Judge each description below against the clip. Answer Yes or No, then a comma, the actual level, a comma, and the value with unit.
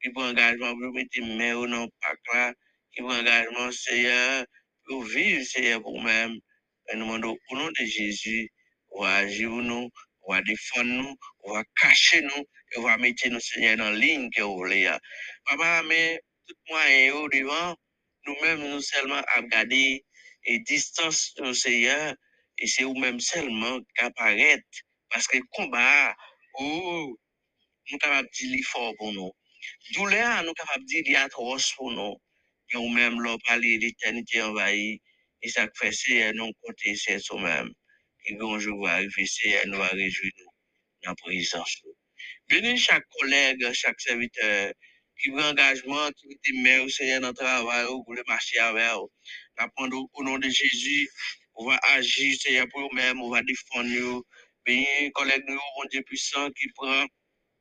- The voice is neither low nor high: No, low, 125 Hz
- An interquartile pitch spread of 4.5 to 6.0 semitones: No, average, 3.2 semitones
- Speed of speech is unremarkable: Yes, average, 180 wpm